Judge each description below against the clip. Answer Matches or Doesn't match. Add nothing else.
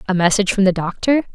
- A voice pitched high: Matches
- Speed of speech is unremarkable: Doesn't match